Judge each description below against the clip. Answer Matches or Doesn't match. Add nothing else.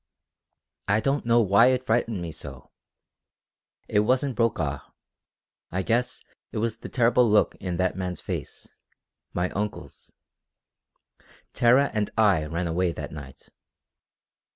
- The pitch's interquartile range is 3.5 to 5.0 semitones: Matches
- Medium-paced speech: Doesn't match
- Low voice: Matches